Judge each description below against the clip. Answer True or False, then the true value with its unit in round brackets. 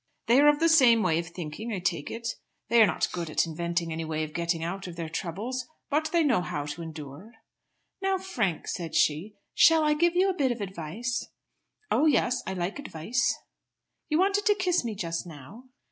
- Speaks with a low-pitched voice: False (200 Hz)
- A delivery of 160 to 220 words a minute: True (205 wpm)